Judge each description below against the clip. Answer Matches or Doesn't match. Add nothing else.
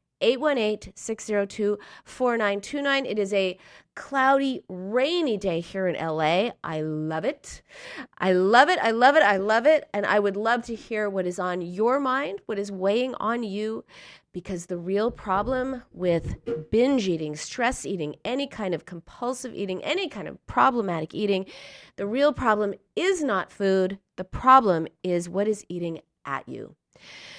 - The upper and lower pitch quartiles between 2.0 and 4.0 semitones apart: Doesn't match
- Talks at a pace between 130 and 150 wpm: Doesn't match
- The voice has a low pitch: Doesn't match